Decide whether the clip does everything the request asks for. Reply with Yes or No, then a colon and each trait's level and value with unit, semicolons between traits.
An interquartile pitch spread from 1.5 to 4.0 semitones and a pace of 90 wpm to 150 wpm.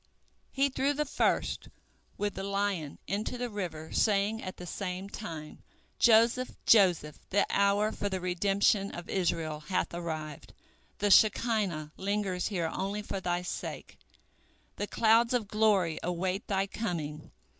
Yes: average, 3.3 semitones; average, 140 wpm